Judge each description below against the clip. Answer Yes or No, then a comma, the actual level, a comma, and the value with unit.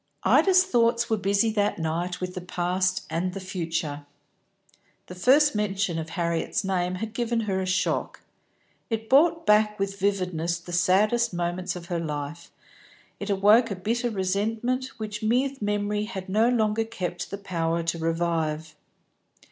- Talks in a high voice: Yes, high, 195 Hz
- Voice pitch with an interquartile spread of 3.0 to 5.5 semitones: Yes, average, 3.9 semitones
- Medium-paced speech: Yes, average, 155 wpm